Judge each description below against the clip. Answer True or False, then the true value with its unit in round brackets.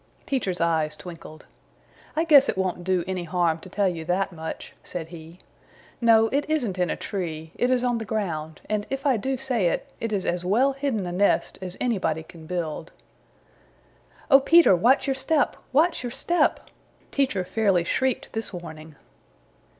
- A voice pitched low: False (190 Hz)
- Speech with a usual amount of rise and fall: False (6.9 semitones)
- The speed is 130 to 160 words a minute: False (175 wpm)